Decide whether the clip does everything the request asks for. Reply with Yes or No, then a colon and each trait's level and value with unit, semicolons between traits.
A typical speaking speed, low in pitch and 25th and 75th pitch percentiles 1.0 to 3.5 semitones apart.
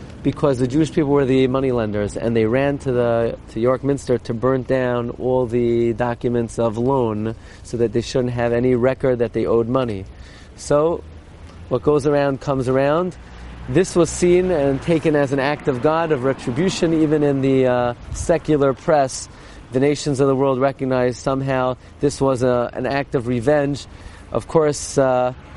Yes: average, 180 wpm; low, 130 Hz; average, 3.2 semitones